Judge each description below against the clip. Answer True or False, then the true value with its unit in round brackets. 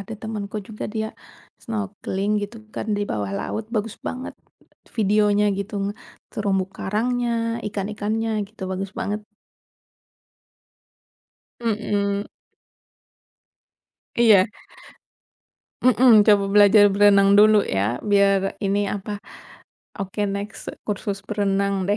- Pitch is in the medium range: False (205 Hz)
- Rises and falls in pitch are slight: True (1.3 semitones)